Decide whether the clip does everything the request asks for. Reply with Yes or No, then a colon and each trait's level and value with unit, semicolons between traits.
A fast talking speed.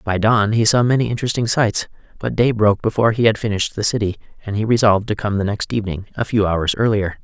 Yes: fast, 230 wpm